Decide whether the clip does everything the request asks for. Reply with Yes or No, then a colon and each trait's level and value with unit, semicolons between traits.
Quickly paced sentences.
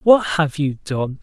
No: average, 195 wpm